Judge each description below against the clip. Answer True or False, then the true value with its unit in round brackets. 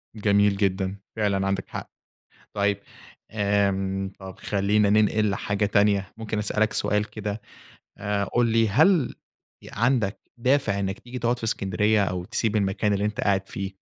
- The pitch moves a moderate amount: False (1.8 semitones)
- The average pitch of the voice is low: True (105 Hz)